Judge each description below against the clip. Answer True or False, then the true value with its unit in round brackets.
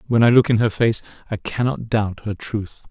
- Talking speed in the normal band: False (225 wpm)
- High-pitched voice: False (110 Hz)